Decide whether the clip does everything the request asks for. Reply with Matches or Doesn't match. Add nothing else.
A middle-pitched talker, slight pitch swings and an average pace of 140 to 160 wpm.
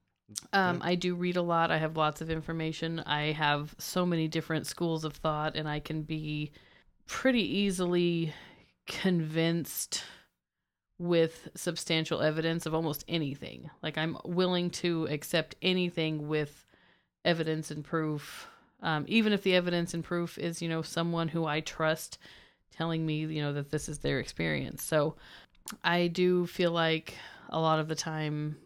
Matches